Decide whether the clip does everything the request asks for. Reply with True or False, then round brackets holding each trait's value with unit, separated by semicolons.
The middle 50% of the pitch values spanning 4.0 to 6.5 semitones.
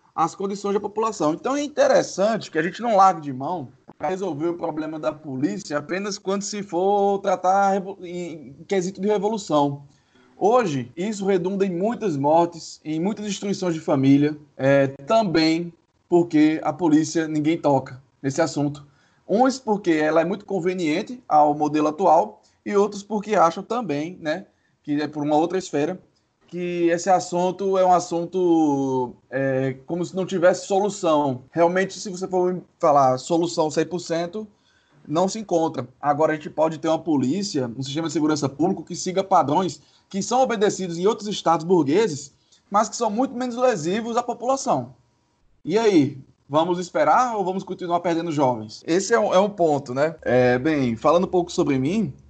True (4.5 semitones)